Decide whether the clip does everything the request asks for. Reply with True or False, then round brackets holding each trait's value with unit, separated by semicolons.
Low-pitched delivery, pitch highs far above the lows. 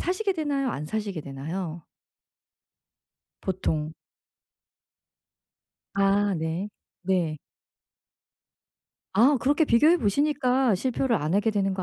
False (205 Hz; 7.6 semitones)